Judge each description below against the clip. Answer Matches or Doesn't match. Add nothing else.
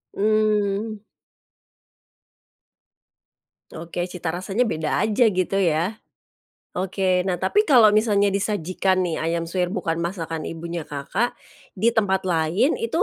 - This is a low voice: Doesn't match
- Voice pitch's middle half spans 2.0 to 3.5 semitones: Doesn't match